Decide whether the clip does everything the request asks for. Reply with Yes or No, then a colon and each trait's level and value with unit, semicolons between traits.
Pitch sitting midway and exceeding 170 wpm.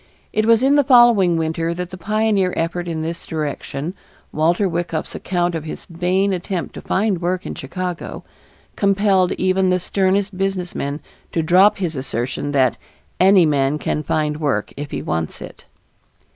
No: medium, 175 Hz; average, 160 wpm